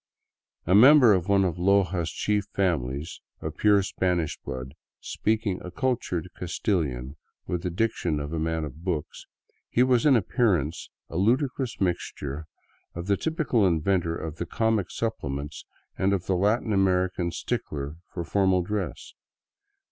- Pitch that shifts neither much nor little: Yes, average, 4.3 semitones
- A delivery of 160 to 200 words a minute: No, average, 145 wpm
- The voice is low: Yes, very low, 90 Hz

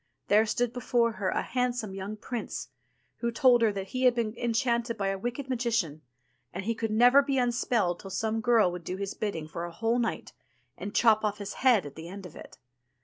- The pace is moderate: No, fast, 215 wpm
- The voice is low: No, high, 225 Hz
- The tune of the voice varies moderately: Yes, average, 3.7 semitones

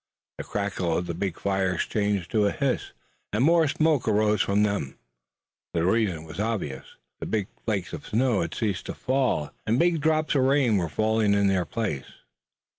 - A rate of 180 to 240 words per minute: Yes, average, 185 wpm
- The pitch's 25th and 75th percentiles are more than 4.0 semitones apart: Yes, average, 4.6 semitones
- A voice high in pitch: No, low, 105 Hz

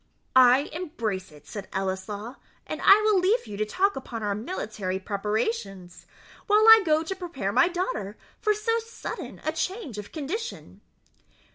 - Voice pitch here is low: No, very high, 270 Hz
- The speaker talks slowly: No, average, 155 wpm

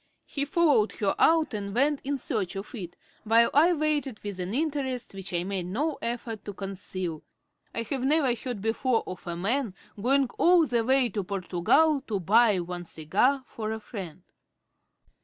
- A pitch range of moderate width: No, wide, 6.0 semitones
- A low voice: No, high, 225 Hz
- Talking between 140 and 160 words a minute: No, average, 175 wpm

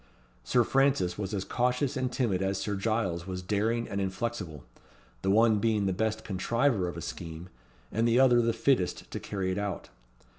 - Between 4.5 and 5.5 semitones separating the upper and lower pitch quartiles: No, average, 3.9 semitones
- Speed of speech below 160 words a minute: No, average, 185 wpm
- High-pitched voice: No, low, 105 Hz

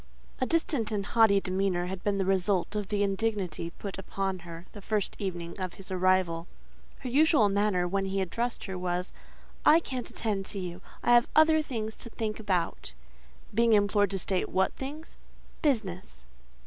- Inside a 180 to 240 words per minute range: No, average, 170 wpm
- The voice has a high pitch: Yes, high, 195 Hz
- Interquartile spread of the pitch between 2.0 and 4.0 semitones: Yes, average, 3.4 semitones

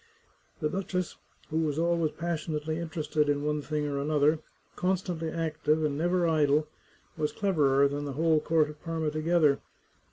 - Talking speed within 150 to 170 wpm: Yes, average, 155 wpm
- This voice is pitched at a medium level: Yes, medium, 155 Hz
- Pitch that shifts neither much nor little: No, narrow, 1.9 semitones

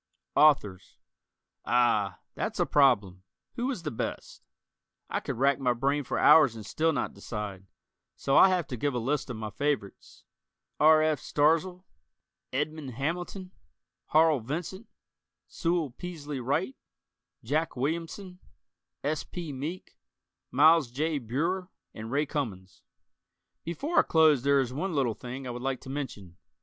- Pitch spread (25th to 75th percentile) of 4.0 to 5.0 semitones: Yes, average, 4.7 semitones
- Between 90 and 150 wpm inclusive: Yes, average, 145 wpm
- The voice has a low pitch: No, medium, 145 Hz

